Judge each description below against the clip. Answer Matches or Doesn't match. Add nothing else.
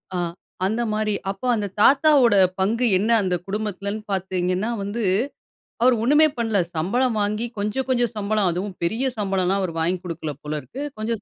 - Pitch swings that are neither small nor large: Matches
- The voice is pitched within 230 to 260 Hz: Doesn't match